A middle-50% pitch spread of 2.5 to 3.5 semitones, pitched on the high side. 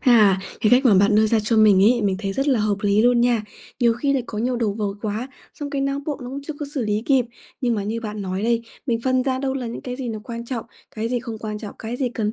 Yes: average, 3.0 semitones; high, 230 Hz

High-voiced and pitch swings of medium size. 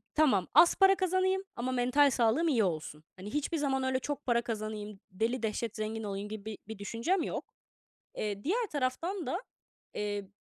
No: high, 240 Hz; wide, 5.9 semitones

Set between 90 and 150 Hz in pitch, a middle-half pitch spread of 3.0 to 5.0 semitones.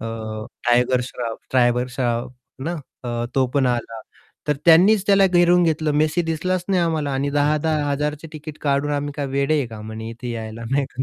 Yes: medium, 140 Hz; average, 4.5 semitones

